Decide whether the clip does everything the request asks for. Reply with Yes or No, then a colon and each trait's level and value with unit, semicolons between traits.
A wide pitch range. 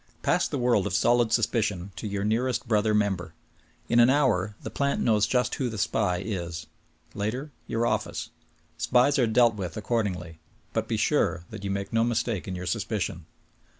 No: average, 3.5 semitones